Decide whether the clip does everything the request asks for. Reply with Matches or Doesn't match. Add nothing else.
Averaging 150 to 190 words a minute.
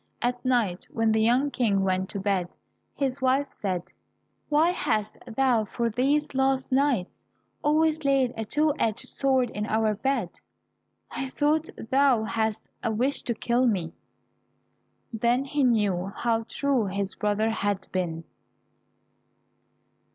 Doesn't match